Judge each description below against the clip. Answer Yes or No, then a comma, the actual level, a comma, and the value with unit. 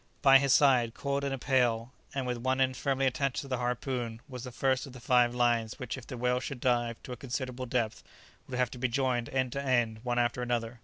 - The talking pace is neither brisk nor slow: No, fast, 245 wpm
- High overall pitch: No, low, 125 Hz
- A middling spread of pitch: No, narrow, 1.7 semitones